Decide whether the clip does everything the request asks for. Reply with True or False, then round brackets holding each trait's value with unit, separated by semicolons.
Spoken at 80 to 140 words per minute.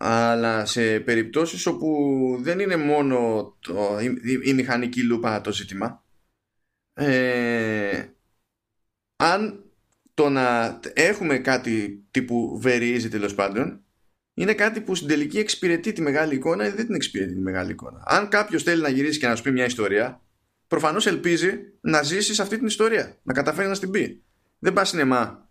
False (160 wpm)